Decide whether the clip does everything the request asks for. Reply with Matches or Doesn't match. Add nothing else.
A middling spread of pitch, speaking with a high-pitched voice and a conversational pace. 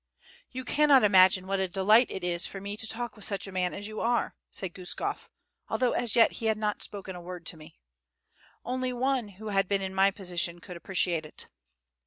Doesn't match